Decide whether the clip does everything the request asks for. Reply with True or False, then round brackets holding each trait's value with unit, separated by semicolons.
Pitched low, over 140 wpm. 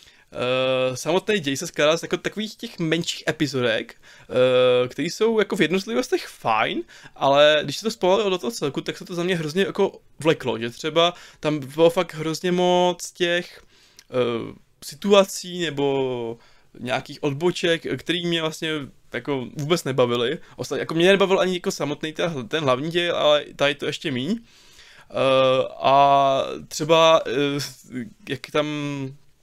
False (160 Hz; 155 wpm)